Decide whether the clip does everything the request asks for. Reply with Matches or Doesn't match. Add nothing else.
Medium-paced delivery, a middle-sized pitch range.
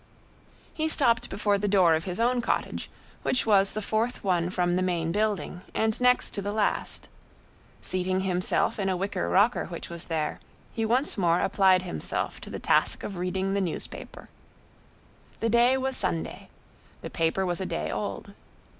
Matches